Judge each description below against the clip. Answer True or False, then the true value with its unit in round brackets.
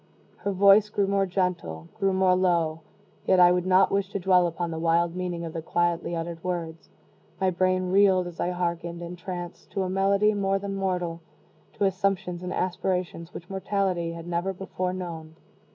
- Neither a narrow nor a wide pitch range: False (2.1 semitones)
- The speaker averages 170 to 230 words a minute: True (180 wpm)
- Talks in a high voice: False (180 Hz)